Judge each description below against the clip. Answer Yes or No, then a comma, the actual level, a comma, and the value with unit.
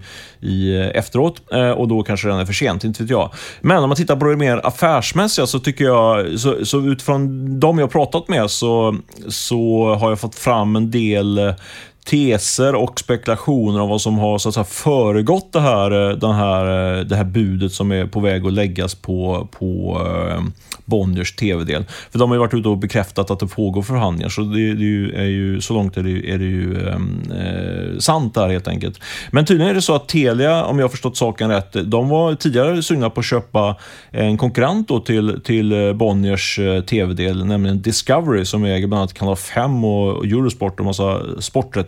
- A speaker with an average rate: No, fast, 200 wpm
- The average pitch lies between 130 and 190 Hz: No, low, 110 Hz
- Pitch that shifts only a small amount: No, average, 4.4 semitones